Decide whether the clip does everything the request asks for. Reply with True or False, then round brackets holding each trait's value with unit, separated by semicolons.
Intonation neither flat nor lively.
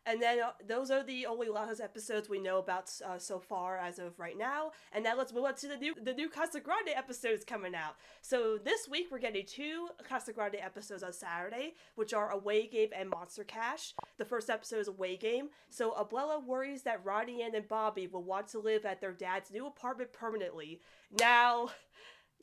True (4.9 semitones)